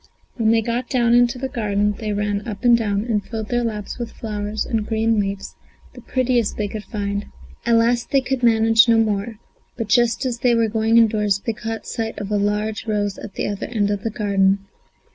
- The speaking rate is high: Yes, fast, 215 wpm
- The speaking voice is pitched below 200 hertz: No, high, 220 Hz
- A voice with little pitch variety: Yes, narrow, 2.2 semitones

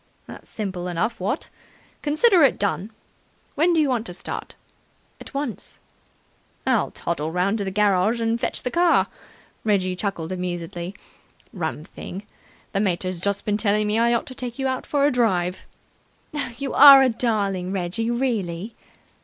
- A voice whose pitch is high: Yes, high, 210 Hz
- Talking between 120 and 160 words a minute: Yes, average, 155 wpm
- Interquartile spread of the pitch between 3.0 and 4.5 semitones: No, average, 4.9 semitones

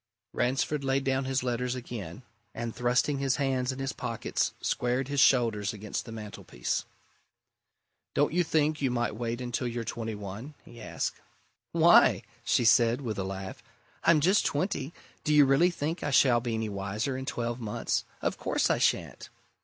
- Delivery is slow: No, average, 170 wpm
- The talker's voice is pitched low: Yes, low, 125 Hz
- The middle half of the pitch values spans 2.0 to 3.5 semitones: Yes, average, 3.1 semitones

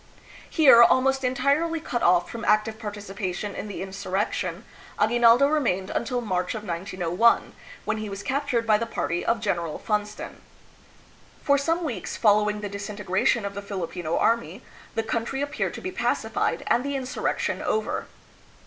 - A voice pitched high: Yes, high, 215 Hz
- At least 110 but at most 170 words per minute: Yes, average, 150 wpm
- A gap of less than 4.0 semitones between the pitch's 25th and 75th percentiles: No, average, 4.3 semitones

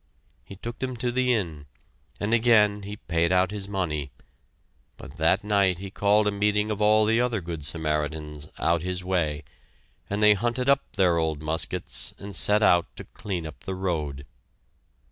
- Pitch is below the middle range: Yes, very low, 95 Hz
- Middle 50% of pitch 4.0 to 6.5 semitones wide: Yes, average, 4.5 semitones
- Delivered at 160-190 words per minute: Yes, average, 175 wpm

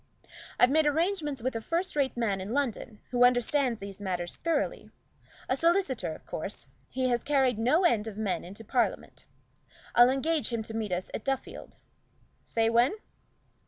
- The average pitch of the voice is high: Yes, high, 245 Hz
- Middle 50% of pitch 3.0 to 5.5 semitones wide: Yes, average, 4.7 semitones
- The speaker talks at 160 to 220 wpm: Yes, average, 165 wpm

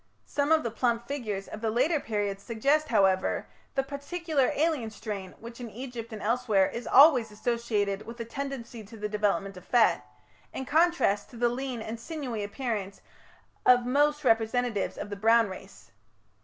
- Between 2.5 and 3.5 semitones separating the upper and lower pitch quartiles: No, average, 4.4 semitones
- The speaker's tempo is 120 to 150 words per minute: No, average, 170 wpm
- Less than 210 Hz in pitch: No, high, 230 Hz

